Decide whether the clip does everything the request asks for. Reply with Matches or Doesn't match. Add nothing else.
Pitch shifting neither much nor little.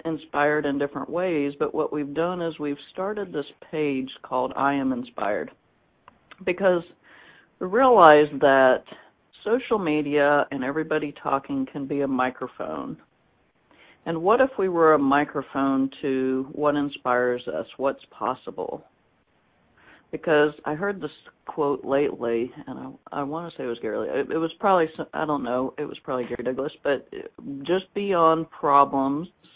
Matches